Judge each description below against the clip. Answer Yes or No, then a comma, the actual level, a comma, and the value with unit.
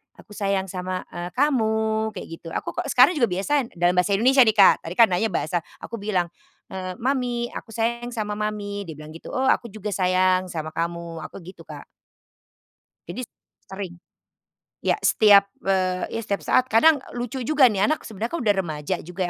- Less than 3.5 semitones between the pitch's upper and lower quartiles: No, average, 4.1 semitones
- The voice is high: Yes, high, 205 Hz